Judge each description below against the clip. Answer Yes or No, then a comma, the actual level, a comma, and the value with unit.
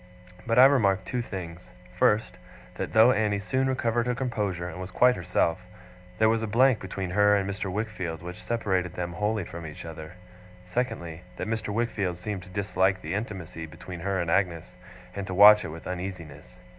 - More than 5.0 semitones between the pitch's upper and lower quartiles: No, average, 3.8 semitones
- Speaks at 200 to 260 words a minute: No, average, 185 wpm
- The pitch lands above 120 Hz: No, very low, 95 Hz